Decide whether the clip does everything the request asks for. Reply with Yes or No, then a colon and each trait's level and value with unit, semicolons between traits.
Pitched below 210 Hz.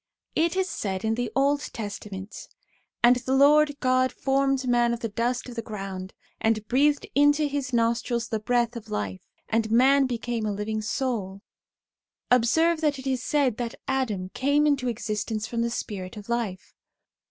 No: high, 240 Hz